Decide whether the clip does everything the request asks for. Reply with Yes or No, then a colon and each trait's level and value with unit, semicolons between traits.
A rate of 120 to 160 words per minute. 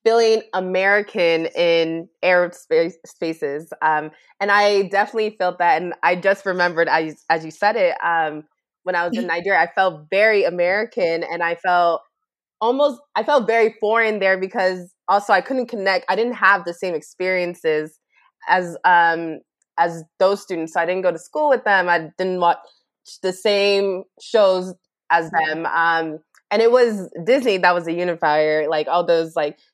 No: average, 170 wpm